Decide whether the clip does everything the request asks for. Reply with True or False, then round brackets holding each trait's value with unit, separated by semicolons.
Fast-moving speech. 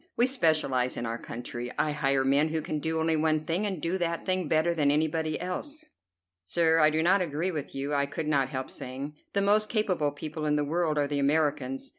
True (220 wpm)